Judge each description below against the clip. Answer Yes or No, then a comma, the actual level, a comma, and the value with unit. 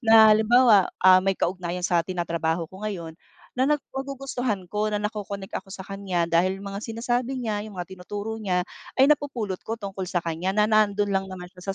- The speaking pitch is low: No, high, 200 Hz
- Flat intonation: No, average, 3.2 semitones